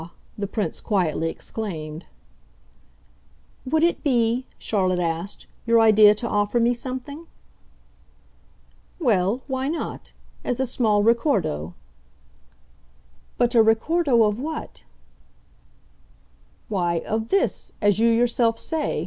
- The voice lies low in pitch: No, high, 225 Hz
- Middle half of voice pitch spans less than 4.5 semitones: Yes, average, 4.0 semitones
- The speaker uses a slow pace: Yes, slow, 105 wpm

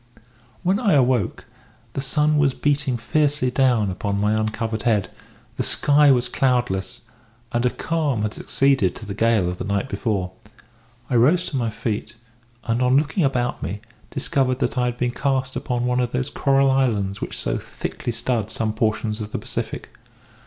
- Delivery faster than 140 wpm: Yes, average, 175 wpm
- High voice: No, low, 125 Hz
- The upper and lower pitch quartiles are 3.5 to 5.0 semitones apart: Yes, average, 3.9 semitones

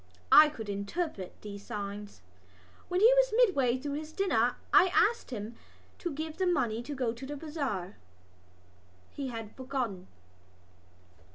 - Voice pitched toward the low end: No, very high, 265 Hz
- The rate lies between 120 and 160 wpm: Yes, average, 150 wpm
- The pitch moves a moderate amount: No, wide, 6.6 semitones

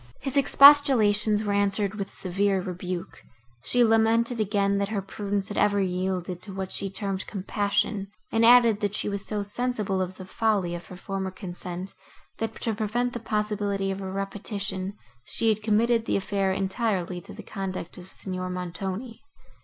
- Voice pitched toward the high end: Yes, high, 200 Hz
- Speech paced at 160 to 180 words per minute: Yes, average, 170 wpm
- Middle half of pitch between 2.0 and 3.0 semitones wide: Yes, narrow, 2.4 semitones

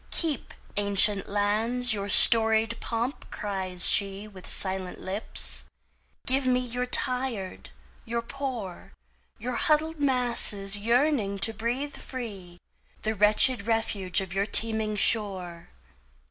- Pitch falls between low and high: No, high, 220 Hz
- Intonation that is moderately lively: Yes, average, 4.0 semitones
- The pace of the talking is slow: Yes, slow, 105 wpm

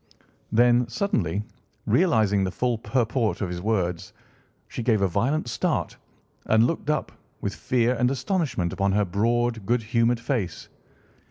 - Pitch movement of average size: Yes, average, 3.6 semitones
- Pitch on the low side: Yes, low, 115 Hz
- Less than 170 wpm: Yes, average, 145 wpm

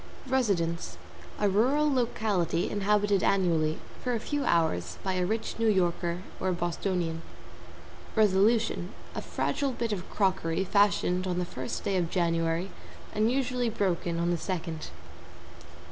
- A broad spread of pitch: No, average, 4.2 semitones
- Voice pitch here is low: No, high, 190 Hz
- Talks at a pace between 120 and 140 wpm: Yes, slow, 135 wpm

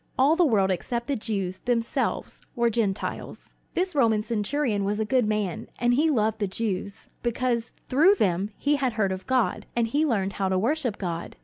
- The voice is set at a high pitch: Yes, high, 225 Hz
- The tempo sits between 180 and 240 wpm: Yes, average, 190 wpm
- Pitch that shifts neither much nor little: Yes, average, 4.3 semitones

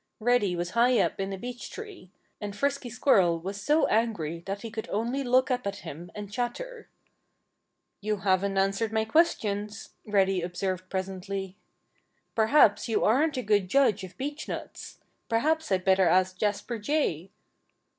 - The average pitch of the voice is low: No, high, 210 Hz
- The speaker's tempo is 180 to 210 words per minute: No, average, 155 wpm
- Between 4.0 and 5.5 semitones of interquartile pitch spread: Yes, average, 4.4 semitones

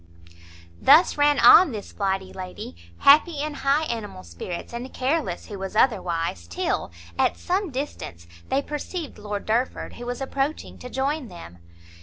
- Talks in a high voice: Yes, high, 245 Hz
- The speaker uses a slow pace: No, average, 150 wpm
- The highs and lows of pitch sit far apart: Yes, wide, 7.3 semitones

